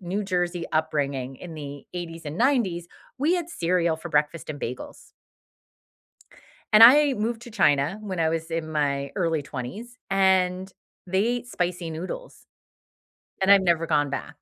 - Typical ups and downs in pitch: Yes, average, 4.3 semitones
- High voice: No, medium, 175 Hz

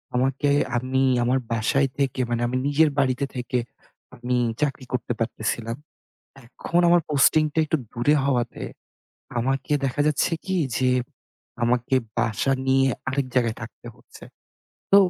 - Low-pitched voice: Yes, low, 130 Hz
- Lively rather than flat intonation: No, narrow, 2.5 semitones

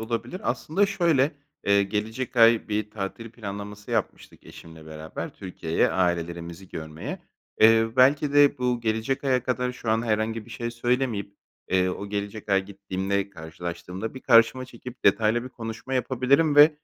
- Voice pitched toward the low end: Yes, low, 110 Hz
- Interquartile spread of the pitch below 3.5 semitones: No, average, 4.3 semitones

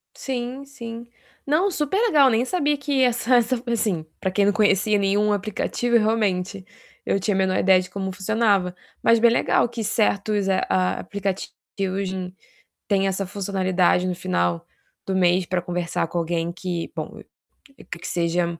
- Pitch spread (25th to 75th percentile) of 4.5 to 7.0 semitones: No, average, 4.1 semitones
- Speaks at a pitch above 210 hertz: No, high, 195 Hz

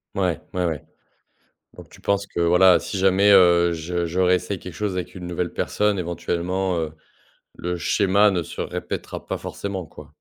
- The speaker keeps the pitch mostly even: Yes, narrow, 1.8 semitones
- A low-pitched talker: Yes, very low, 90 Hz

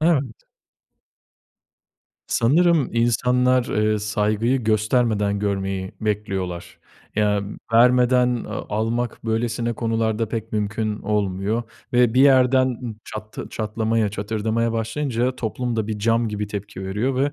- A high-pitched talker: No, low, 115 Hz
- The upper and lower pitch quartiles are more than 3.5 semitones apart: No, average, 2.7 semitones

